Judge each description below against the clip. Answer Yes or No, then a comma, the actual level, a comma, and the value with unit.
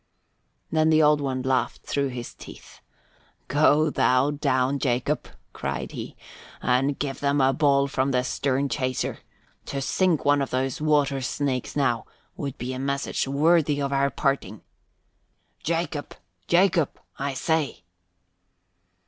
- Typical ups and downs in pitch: No, narrow, 2.1 semitones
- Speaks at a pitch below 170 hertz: Yes, medium, 140 Hz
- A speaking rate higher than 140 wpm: No, slow, 135 wpm